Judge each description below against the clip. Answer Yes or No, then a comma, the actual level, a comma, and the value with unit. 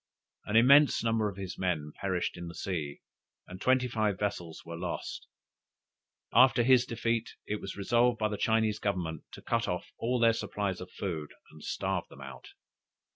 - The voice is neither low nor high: No, low, 105 Hz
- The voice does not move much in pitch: No, average, 4.4 semitones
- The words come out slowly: No, average, 175 wpm